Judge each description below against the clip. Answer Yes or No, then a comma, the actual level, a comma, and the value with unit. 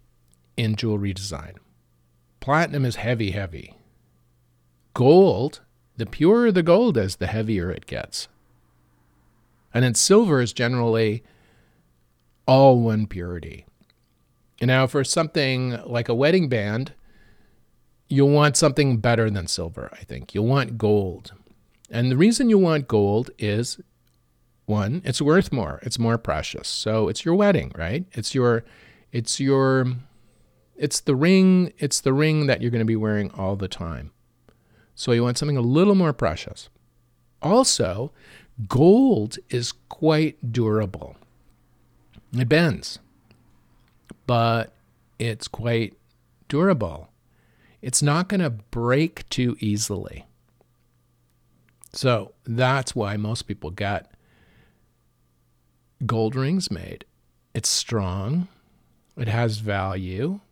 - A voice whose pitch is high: No, low, 115 Hz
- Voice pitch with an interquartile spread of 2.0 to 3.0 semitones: No, average, 4.8 semitones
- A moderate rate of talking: No, slow, 120 wpm